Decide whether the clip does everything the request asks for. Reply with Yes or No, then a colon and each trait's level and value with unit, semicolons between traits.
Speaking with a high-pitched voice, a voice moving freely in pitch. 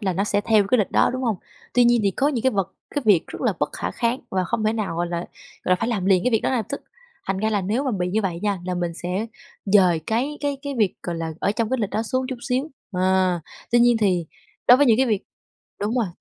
No: high, 210 Hz; average, 4.6 semitones